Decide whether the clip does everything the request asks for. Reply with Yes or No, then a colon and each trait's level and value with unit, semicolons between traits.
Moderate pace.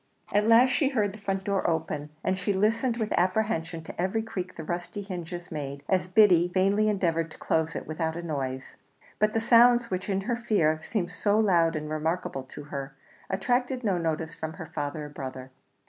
Yes: average, 195 wpm